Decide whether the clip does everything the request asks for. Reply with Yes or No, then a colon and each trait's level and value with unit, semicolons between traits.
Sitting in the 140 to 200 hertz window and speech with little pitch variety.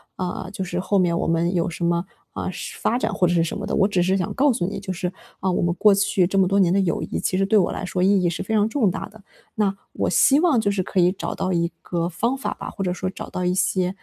Yes: medium, 185 Hz; narrow, 2.3 semitones